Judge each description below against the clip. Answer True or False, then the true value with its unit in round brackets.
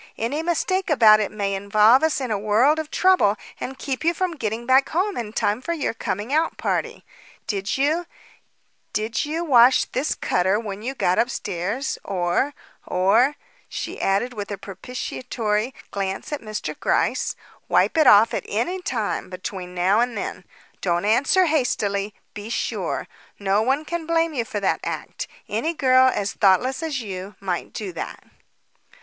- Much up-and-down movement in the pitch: True (6.2 semitones)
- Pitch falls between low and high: False (230 Hz)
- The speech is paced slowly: False (165 wpm)